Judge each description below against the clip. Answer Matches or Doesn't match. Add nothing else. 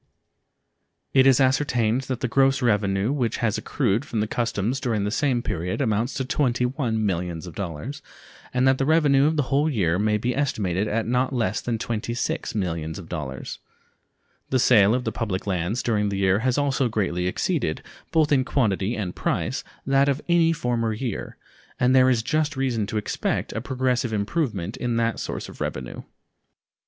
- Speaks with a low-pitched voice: Matches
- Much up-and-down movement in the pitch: Doesn't match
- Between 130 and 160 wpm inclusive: Doesn't match